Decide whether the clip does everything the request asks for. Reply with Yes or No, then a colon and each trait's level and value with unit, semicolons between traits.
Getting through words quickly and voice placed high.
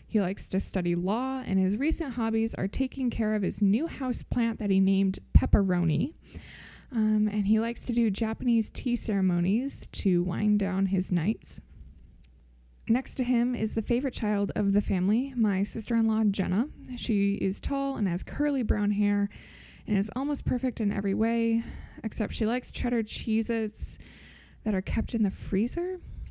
No: average, 175 wpm; high, 215 Hz